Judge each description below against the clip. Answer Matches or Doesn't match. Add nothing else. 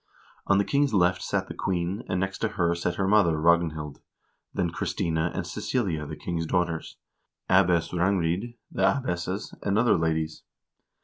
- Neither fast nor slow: Matches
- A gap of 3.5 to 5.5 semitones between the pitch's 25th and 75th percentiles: Doesn't match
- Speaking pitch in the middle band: Doesn't match